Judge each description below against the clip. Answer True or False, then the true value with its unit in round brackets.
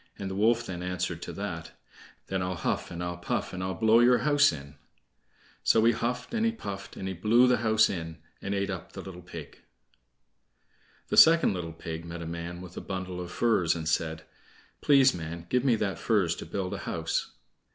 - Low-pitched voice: True (95 Hz)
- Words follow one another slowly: False (205 wpm)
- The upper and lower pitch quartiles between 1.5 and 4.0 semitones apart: False (4.8 semitones)